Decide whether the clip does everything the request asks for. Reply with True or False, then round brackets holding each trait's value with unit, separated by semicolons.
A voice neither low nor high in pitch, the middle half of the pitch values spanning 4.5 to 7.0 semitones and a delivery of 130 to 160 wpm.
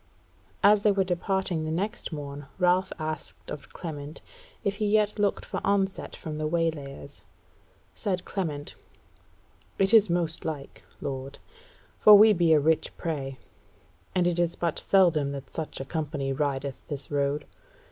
True (160 Hz; 4.8 semitones; 150 wpm)